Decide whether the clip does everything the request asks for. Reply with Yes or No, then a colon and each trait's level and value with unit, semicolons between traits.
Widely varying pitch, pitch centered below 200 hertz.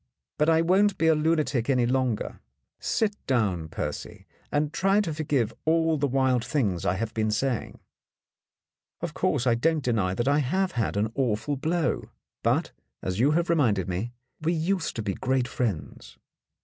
Yes: wide, 6.1 semitones; low, 135 Hz